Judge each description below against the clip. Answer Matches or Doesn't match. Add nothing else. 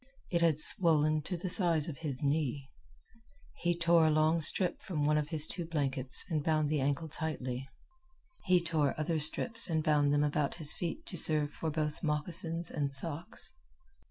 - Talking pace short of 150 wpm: Doesn't match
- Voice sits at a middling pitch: Matches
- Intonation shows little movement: Matches